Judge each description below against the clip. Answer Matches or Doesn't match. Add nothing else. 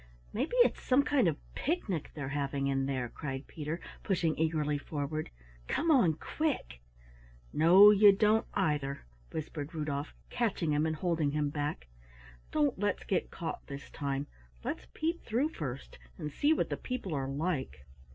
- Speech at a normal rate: Matches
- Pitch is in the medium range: Matches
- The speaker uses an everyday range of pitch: Doesn't match